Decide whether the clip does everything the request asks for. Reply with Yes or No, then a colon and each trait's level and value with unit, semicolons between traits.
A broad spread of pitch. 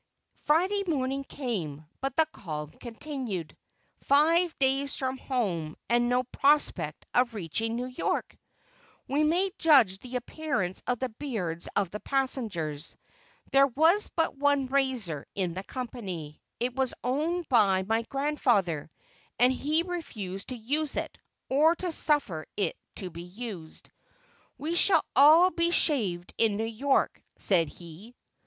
Yes: wide, 7.1 semitones